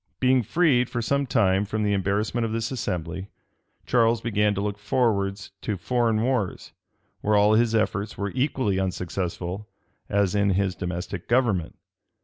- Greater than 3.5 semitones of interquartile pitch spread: No, average, 3.2 semitones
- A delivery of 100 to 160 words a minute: Yes, average, 145 wpm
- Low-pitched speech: Yes, low, 105 Hz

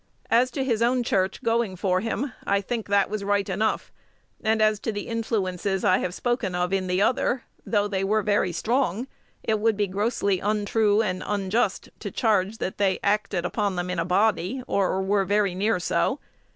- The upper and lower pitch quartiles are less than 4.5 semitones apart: Yes, average, 2.8 semitones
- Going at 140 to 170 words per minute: No, average, 190 wpm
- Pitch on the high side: Yes, high, 205 Hz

